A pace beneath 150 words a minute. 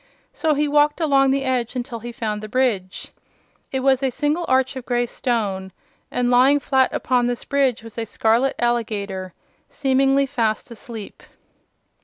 No: average, 160 wpm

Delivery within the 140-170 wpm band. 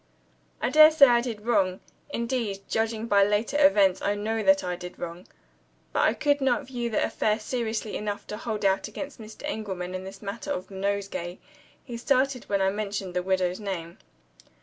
No: average, 185 wpm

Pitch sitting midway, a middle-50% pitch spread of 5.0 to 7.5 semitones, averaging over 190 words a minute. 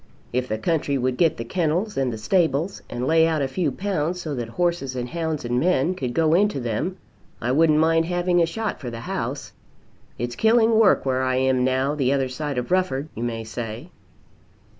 Yes: medium, 145 Hz; wide, 5.4 semitones; fast, 205 wpm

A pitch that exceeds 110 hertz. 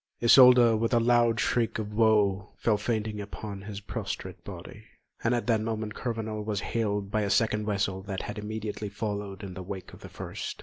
No: low, 105 Hz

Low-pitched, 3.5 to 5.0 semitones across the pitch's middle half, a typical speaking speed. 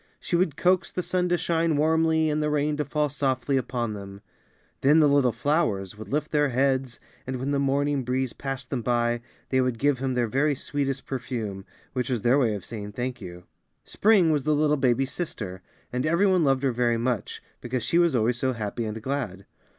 No: low, 130 Hz; average, 3.9 semitones; fast, 210 wpm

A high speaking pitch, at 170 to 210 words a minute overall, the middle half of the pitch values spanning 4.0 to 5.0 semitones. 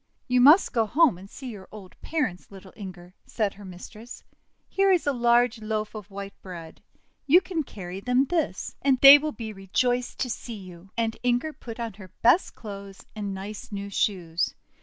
Yes: high, 215 Hz; average, 185 wpm; average, 4.4 semitones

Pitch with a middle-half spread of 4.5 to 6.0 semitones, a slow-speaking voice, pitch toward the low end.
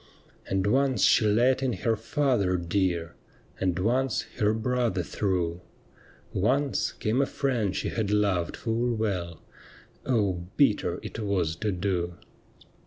Yes: average, 4.9 semitones; slow, 130 wpm; low, 105 Hz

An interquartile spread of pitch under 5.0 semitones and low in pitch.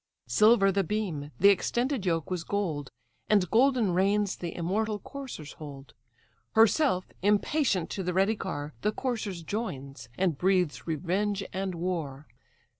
No: average, 4.3 semitones; high, 190 Hz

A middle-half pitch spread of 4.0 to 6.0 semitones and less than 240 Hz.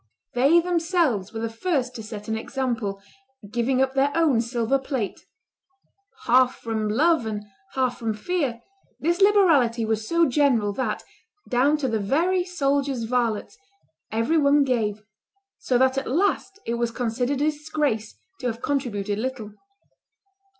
No: average, 4.6 semitones; very high, 255 Hz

